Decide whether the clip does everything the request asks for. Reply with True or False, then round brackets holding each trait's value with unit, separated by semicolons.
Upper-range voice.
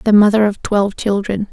True (205 Hz)